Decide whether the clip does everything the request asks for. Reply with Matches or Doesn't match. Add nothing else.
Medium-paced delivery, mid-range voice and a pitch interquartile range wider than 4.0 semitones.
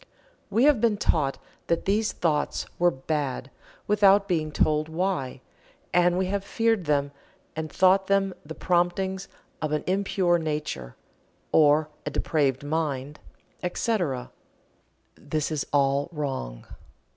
Doesn't match